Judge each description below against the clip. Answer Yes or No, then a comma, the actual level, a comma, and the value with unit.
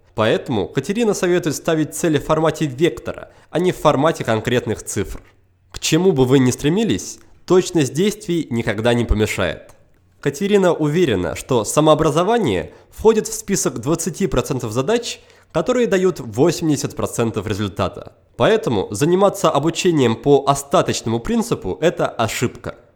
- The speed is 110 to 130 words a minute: Yes, average, 120 wpm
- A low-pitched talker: No, medium, 150 Hz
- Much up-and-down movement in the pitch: Yes, wide, 7.5 semitones